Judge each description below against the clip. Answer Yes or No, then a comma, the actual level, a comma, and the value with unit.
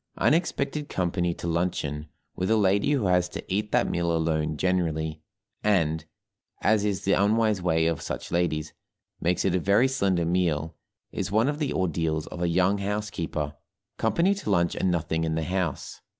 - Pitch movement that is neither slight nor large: Yes, average, 3.9 semitones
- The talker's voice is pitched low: Yes, very low, 90 Hz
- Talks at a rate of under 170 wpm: No, average, 175 wpm